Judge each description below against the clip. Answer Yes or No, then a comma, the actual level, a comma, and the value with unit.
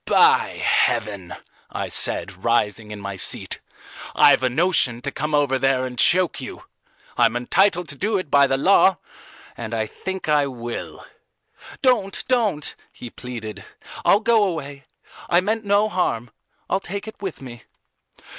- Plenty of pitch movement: Yes, wide, 8.0 semitones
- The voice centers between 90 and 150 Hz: Yes, medium, 140 Hz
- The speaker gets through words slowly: No, average, 155 wpm